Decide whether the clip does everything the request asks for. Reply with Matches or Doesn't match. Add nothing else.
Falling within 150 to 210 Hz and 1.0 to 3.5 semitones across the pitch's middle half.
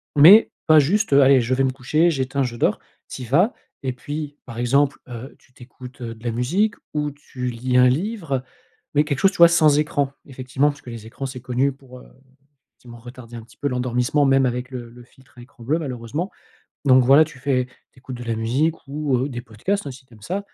Doesn't match